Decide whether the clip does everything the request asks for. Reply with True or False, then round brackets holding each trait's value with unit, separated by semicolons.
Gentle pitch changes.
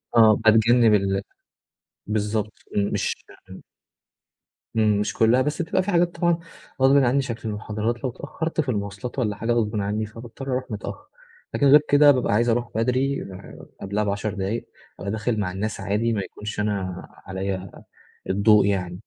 False (3.7 semitones)